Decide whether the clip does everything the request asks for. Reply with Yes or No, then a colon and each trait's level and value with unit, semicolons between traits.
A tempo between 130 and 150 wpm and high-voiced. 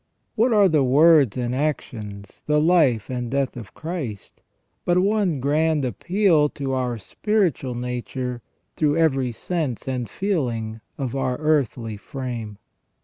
No: slow, 135 wpm; low, 135 Hz